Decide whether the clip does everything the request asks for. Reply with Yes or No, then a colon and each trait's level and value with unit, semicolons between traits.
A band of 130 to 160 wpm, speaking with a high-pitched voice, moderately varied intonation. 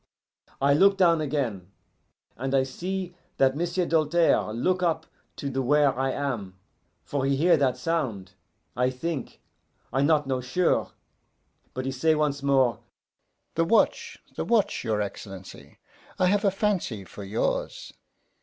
No: average, 145 wpm; medium, 140 Hz; average, 4.9 semitones